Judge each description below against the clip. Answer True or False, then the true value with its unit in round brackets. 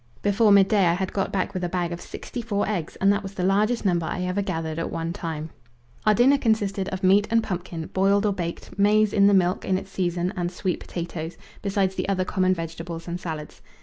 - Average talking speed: False (225 wpm)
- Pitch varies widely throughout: False (2.7 semitones)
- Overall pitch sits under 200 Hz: True (185 Hz)